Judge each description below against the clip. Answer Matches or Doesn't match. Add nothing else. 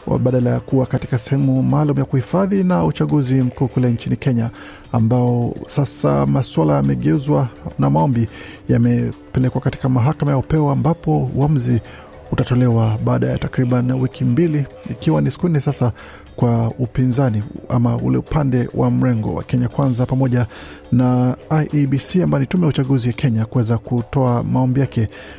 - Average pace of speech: Doesn't match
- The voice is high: Doesn't match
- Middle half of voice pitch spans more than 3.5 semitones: Doesn't match